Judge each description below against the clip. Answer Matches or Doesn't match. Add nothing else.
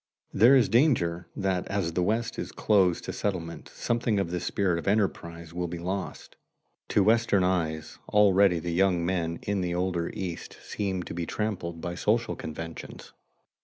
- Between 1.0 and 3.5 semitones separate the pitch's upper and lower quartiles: Matches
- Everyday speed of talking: Matches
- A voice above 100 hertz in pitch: Doesn't match